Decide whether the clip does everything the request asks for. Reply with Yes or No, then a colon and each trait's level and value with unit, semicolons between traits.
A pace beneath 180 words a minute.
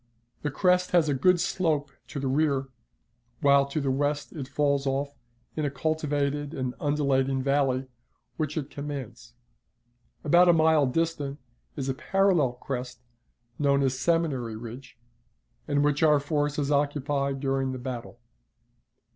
Yes: average, 140 wpm